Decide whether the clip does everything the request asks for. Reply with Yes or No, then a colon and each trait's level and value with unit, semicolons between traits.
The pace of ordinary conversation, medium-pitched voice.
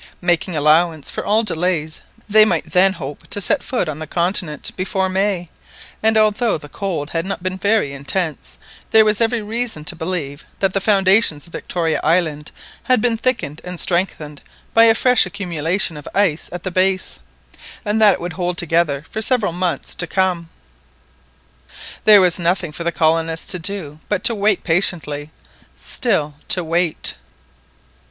Yes: average, 165 wpm; medium, 180 Hz